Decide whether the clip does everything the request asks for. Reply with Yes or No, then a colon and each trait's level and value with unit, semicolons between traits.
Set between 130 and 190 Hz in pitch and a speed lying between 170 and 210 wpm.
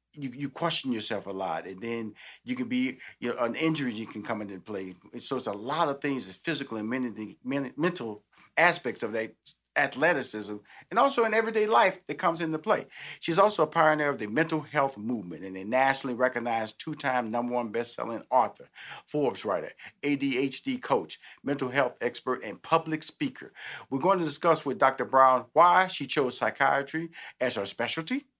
Yes: low, 135 Hz; average, 185 wpm